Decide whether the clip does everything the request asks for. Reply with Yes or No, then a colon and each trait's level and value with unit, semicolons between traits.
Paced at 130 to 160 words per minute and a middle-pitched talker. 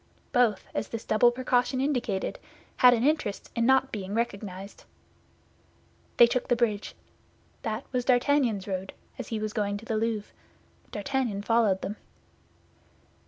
No: average, 140 wpm; high, 230 Hz